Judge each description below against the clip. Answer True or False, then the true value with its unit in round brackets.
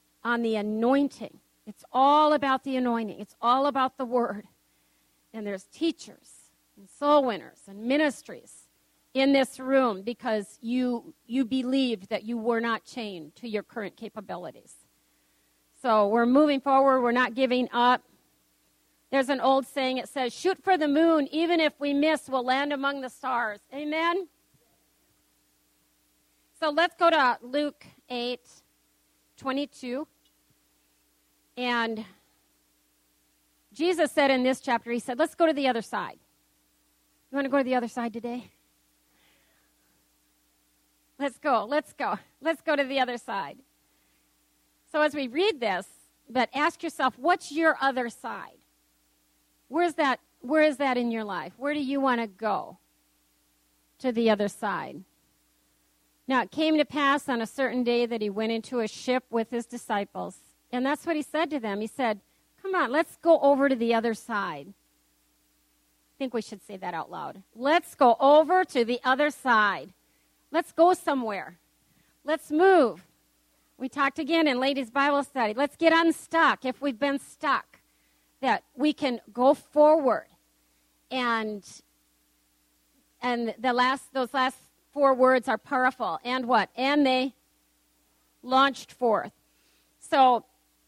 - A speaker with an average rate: True (150 wpm)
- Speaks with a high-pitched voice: True (245 Hz)